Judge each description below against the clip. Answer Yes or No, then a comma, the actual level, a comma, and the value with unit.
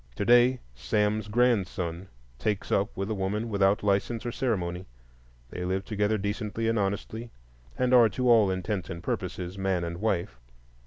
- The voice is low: Yes, low, 100 Hz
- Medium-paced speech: Yes, average, 160 wpm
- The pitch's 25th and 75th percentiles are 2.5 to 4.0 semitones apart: Yes, average, 3.1 semitones